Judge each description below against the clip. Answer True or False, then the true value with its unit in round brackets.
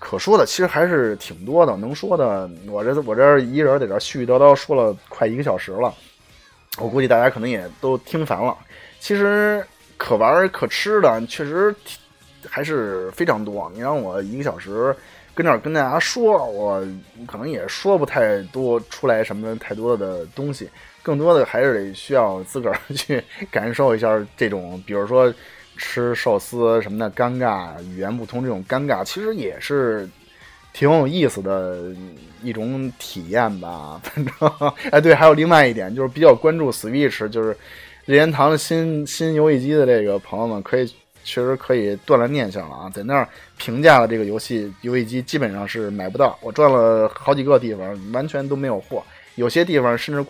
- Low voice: True (125 Hz)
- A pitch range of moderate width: False (5.8 semitones)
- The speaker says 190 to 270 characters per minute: False (280 characters per minute)